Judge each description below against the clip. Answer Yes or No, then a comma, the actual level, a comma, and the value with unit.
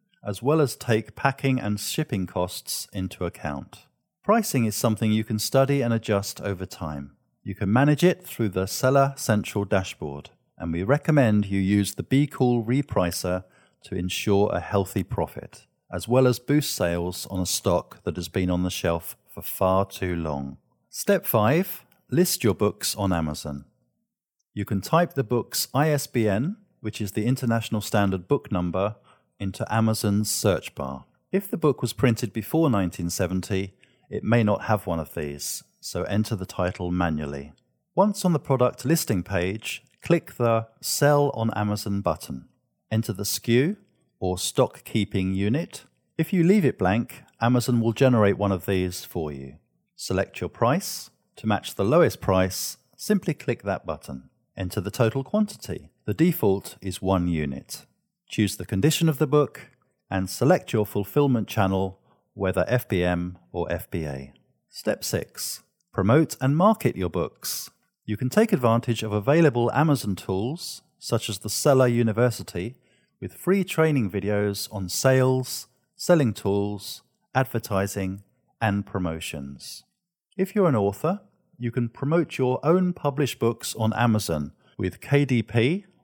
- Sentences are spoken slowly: No, average, 150 wpm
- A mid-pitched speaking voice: No, low, 110 Hz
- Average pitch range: No, wide, 6.2 semitones